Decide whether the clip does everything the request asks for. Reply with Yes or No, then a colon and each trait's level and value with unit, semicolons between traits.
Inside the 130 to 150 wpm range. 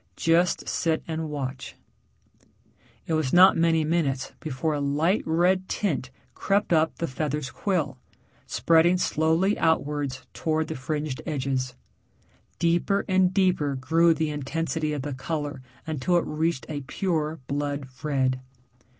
Yes: slow, 135 wpm